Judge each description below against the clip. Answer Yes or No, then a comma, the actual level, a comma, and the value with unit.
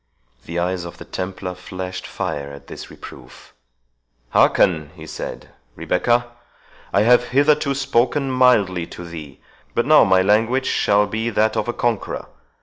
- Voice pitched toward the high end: No, low, 100 Hz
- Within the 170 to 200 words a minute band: No, average, 145 wpm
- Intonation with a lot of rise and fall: Yes, wide, 5.9 semitones